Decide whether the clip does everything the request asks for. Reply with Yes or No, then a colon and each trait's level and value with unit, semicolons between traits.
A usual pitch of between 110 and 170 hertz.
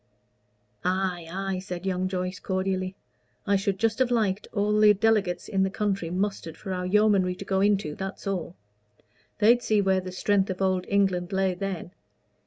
No: high, 190 Hz